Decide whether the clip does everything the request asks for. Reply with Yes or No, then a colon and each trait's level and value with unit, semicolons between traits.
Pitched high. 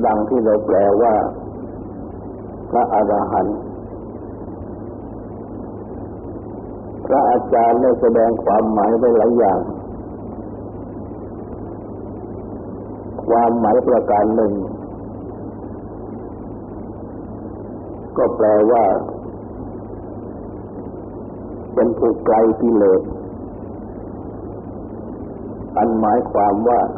No: low, 105 Hz